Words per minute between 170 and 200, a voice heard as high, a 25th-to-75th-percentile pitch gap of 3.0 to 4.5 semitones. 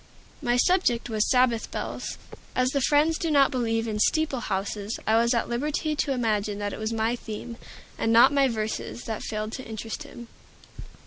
Yes: average, 185 wpm; high, 235 Hz; average, 3.8 semitones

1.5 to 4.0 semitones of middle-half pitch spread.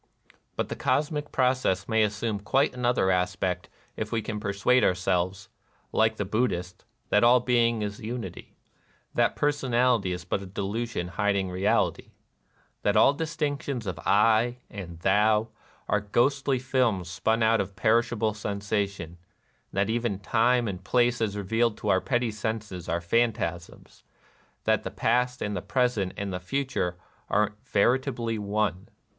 Yes: average, 3.7 semitones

